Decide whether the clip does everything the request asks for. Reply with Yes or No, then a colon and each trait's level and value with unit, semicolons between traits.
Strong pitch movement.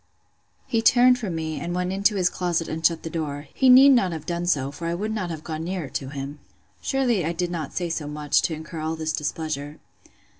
No: average, 3.1 semitones